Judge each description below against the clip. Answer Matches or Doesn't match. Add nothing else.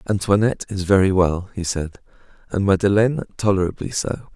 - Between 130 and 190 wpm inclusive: Matches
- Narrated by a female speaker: Doesn't match